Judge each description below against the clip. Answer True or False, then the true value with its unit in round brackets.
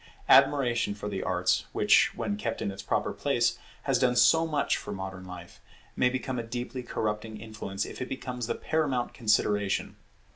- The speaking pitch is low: True (115 Hz)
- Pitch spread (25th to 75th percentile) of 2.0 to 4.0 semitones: True (3.7 semitones)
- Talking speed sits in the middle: True (175 wpm)